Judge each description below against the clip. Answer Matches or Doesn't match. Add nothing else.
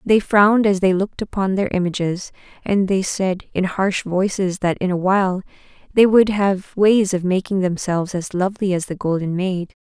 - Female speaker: Matches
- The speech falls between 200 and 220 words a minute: Doesn't match